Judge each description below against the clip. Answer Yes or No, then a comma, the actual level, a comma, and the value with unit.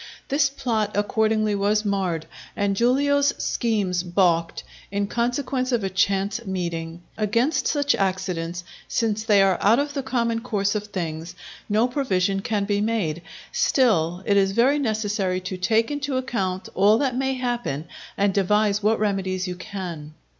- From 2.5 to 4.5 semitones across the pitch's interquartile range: Yes, average, 4.0 semitones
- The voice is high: Yes, high, 205 Hz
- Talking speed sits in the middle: Yes, average, 155 wpm